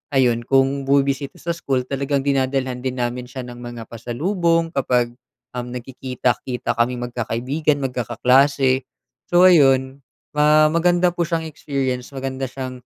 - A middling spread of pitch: No, narrow, 2.3 semitones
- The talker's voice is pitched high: No, low, 135 Hz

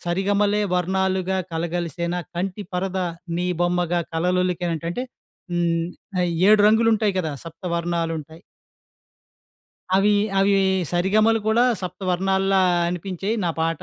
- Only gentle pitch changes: Yes, narrow, 2.2 semitones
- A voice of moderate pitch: Yes, medium, 180 Hz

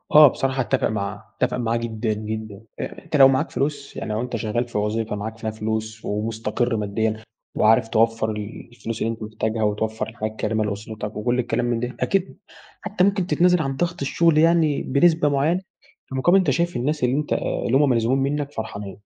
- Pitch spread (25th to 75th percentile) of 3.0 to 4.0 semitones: No, average, 4.6 semitones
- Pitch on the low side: Yes, low, 115 Hz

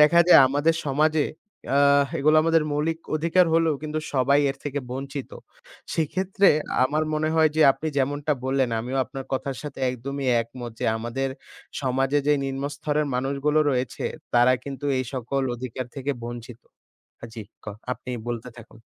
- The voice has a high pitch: No, medium, 140 Hz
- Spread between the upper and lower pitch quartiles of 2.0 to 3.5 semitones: Yes, average, 3.0 semitones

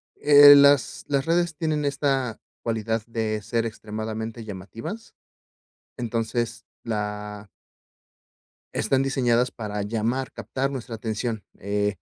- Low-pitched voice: Yes, low, 115 Hz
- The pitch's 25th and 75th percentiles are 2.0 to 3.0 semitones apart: No, average, 3.9 semitones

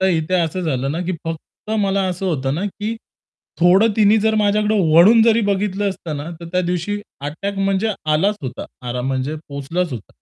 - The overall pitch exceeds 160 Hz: Yes, medium, 185 Hz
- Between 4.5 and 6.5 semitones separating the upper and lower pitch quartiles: Yes, average, 4.8 semitones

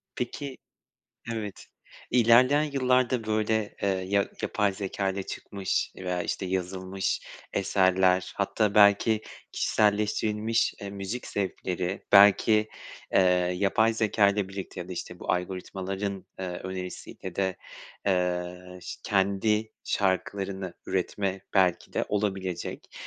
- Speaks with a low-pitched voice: Yes, low, 100 Hz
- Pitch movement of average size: No, narrow, 2.2 semitones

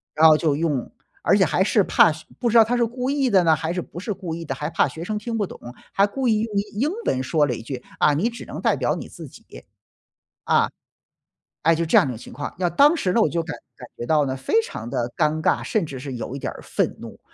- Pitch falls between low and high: Yes, medium, 170 Hz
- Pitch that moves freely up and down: Yes, wide, 6.9 semitones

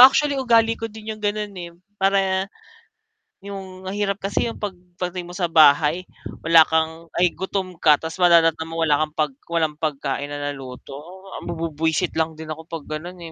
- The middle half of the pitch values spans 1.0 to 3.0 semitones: No, average, 3.4 semitones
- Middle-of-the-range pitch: Yes, medium, 165 Hz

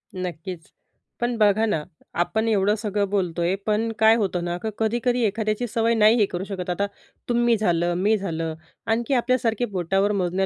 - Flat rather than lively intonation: No, average, 3.6 semitones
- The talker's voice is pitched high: Yes, high, 210 Hz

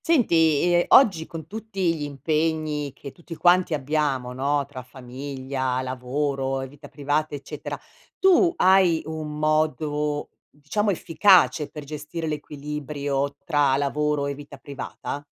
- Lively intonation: No, narrow, 2.4 semitones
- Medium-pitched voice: Yes, medium, 150 Hz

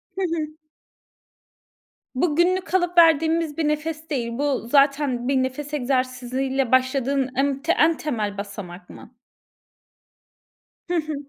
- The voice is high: Yes, very high, 280 Hz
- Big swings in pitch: No, average, 3.7 semitones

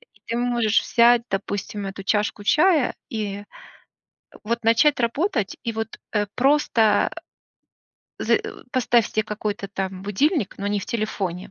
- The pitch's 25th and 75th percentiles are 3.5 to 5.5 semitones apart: No, average, 3.0 semitones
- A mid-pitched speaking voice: No, high, 220 Hz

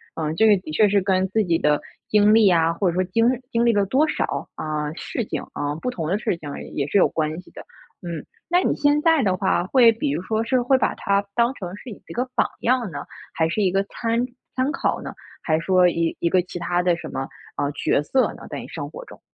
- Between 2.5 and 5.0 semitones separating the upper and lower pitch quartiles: No, wide, 5.6 semitones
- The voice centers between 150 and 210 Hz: Yes, high, 190 Hz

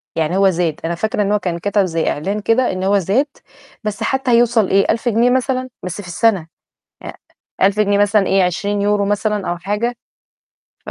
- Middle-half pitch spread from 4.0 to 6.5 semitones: No, average, 3.3 semitones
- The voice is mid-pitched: No, high, 205 Hz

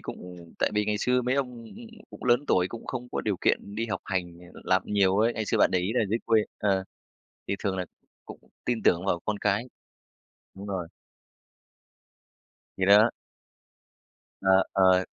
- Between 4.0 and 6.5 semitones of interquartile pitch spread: No, average, 3.4 semitones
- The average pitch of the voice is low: Yes, low, 100 Hz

